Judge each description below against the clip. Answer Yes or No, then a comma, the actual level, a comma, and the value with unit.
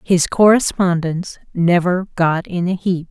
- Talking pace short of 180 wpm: Yes, slow, 135 wpm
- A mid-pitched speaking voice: Yes, medium, 180 Hz